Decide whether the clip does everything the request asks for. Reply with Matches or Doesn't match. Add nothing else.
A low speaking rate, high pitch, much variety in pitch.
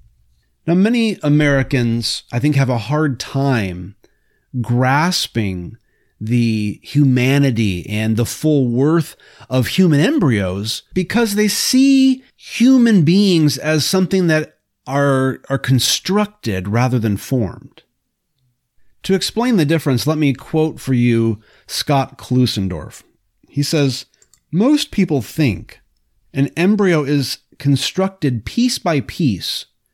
Doesn't match